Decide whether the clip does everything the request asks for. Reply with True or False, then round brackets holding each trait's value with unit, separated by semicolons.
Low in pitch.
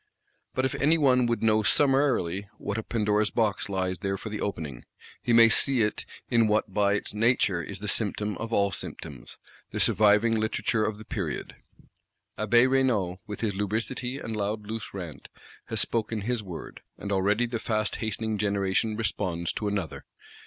True (105 Hz)